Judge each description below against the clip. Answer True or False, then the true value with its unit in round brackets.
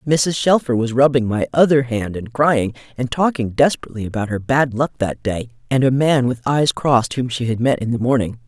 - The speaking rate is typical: False (220 wpm)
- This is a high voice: False (125 Hz)